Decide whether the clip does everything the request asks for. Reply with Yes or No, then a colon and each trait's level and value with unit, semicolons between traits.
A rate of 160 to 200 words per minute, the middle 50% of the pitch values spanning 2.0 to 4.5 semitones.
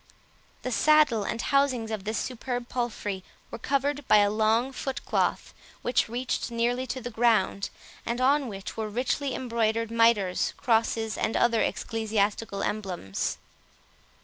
No: average, 140 wpm; average, 2.7 semitones